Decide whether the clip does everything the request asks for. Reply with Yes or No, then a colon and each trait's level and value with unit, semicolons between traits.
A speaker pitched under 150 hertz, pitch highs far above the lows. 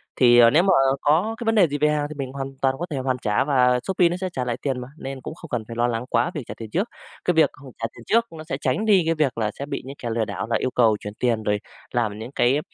No: low, 135 Hz; average, 4.9 semitones